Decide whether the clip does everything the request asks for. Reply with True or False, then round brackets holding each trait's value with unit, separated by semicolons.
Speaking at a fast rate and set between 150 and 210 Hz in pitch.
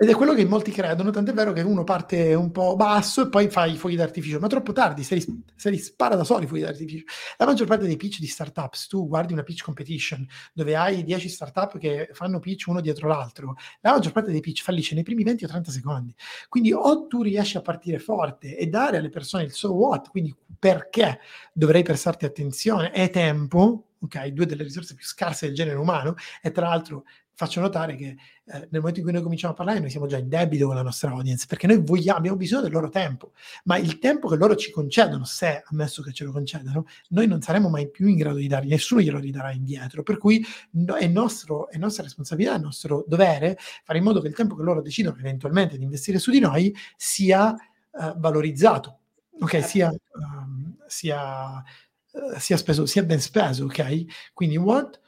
True (215 wpm; 170 Hz)